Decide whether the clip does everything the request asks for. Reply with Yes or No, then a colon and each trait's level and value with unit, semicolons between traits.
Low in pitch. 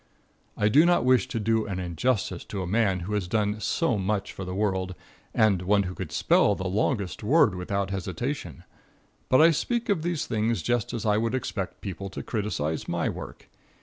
Yes: low, 105 Hz